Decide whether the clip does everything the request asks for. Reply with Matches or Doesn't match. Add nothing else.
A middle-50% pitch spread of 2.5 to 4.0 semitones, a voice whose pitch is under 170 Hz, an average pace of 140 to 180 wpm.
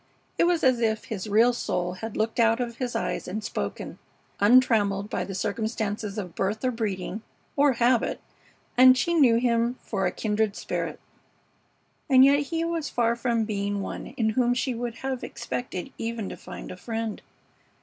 Doesn't match